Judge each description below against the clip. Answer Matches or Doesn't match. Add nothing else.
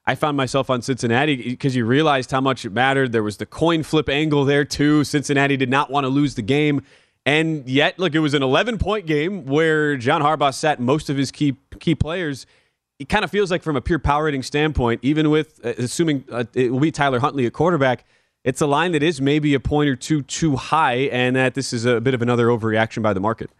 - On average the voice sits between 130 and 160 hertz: Matches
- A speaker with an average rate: Doesn't match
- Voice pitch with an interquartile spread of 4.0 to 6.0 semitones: Doesn't match